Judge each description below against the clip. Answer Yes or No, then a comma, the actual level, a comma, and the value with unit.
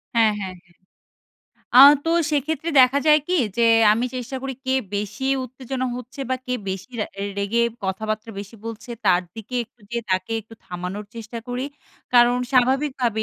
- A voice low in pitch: No, high, 235 Hz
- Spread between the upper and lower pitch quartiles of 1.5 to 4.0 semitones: Yes, average, 3.6 semitones